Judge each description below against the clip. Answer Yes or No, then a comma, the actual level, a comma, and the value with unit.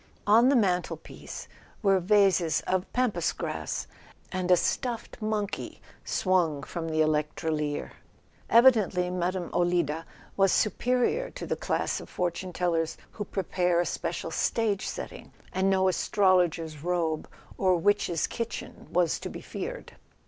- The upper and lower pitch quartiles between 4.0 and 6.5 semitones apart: No, average, 3.2 semitones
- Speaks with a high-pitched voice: No, medium, 180 Hz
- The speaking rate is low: Yes, slow, 130 wpm